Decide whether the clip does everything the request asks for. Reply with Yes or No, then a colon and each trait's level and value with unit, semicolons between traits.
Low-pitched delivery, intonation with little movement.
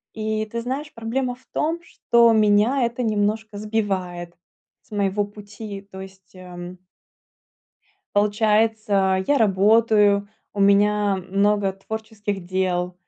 No: high, 210 Hz; narrow, 2.3 semitones